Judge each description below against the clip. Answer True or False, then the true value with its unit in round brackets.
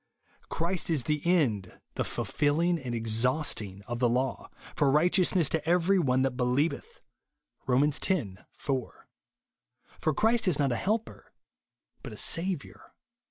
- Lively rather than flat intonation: True (5.8 semitones)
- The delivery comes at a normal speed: True (145 wpm)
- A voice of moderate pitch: True (145 Hz)